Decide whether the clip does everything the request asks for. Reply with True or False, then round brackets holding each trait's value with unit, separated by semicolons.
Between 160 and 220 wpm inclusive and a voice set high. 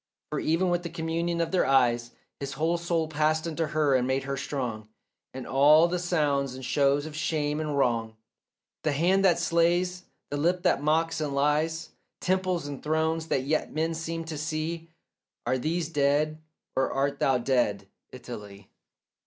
False (170 wpm; 155 Hz)